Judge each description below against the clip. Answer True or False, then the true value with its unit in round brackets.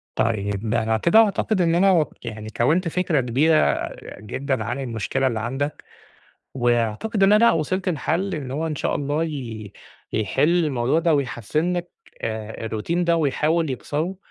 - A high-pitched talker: False (145 Hz)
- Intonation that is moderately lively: False (6.4 semitones)